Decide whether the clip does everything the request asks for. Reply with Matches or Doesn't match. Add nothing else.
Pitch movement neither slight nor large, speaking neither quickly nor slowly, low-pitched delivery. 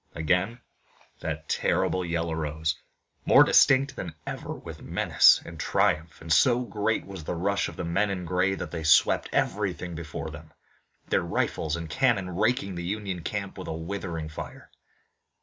Matches